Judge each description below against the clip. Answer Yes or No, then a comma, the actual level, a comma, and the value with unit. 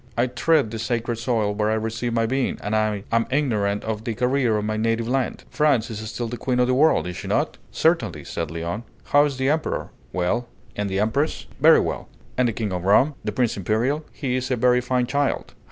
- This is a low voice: Yes, low, 115 Hz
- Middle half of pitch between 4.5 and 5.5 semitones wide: No, average, 3.2 semitones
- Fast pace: Yes, fast, 225 wpm